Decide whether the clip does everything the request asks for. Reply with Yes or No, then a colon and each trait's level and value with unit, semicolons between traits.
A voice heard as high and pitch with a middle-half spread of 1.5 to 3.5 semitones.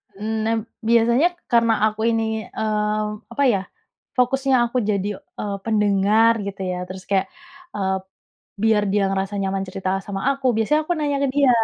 Yes: high, 215 Hz; average, 3.0 semitones